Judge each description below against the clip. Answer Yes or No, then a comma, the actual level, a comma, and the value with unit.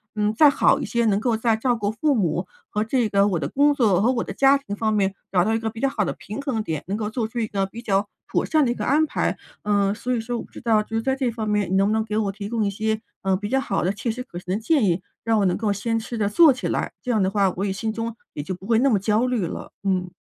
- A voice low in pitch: No, high, 220 Hz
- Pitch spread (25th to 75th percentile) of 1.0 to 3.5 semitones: Yes, average, 3.1 semitones